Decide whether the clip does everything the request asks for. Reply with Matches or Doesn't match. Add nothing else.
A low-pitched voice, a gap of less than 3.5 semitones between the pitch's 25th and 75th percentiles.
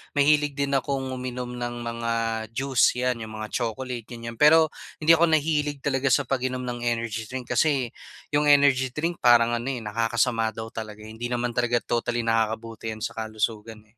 Matches